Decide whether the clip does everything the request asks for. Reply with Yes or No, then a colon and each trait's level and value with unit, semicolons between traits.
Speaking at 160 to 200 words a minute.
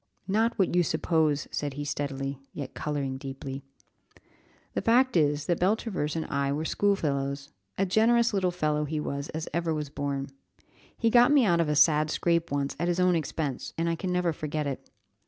Yes: average, 190 wpm